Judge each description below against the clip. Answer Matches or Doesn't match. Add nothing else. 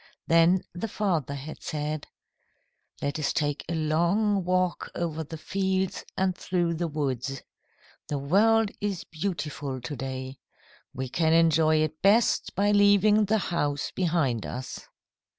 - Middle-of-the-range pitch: Matches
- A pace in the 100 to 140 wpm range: Matches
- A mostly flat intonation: Doesn't match